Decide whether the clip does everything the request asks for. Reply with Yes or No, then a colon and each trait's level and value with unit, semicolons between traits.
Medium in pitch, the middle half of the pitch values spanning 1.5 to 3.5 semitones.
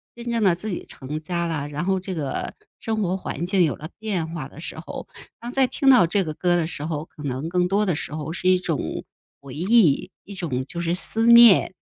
No: medium, 175 Hz; average, 4.3 semitones